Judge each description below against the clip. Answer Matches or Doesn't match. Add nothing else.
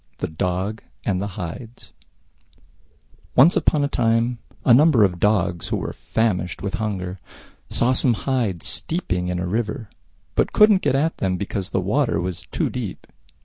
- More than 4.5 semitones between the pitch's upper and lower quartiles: Matches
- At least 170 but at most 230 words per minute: Doesn't match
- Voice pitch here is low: Matches